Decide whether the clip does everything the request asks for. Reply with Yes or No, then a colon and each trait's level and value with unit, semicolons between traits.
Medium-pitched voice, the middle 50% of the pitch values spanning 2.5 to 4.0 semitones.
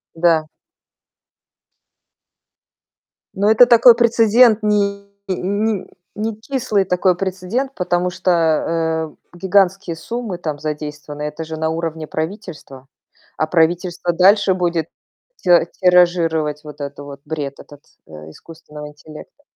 No: medium, 175 Hz; average, 4.4 semitones